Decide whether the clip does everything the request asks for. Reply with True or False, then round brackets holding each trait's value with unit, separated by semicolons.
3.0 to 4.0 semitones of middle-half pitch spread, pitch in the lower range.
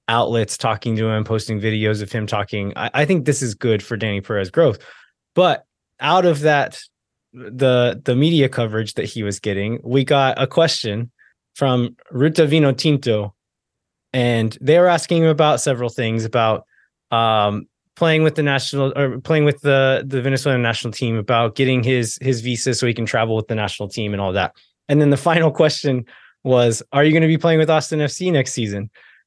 False (4.6 semitones; 125 Hz)